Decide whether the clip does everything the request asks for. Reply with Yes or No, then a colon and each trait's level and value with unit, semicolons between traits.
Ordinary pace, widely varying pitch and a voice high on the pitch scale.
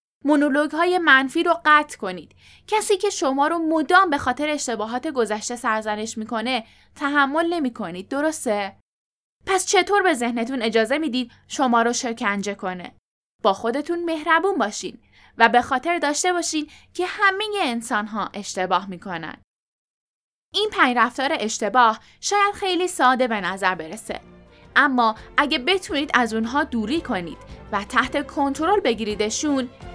Yes: average, 130 wpm; wide, 6.5 semitones; very high, 265 Hz